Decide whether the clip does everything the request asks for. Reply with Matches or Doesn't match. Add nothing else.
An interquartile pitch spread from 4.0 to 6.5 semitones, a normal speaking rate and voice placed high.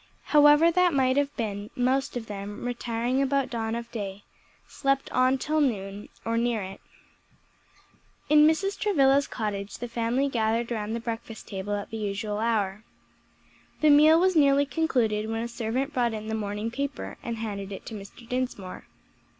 Matches